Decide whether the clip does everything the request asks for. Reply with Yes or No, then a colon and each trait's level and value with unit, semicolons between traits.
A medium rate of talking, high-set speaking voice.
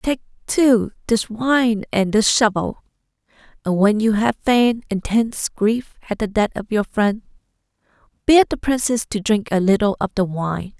Yes: average, 165 wpm; high, 220 Hz